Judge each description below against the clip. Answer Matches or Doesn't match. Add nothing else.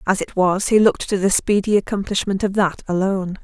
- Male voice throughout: Doesn't match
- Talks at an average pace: Doesn't match